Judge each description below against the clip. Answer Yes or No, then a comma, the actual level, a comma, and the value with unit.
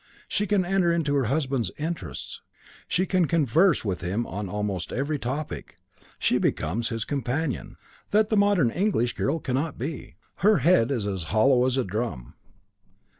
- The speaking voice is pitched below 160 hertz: Yes, low, 135 Hz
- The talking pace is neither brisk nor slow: Yes, average, 160 wpm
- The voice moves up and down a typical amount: No, wide, 6.8 semitones